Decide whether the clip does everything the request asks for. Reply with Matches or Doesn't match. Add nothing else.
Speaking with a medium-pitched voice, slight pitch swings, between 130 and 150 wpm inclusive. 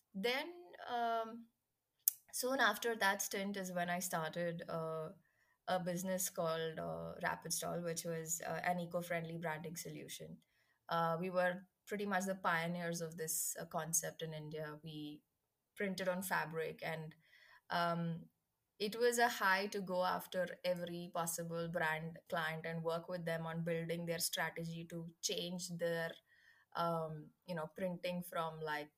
Matches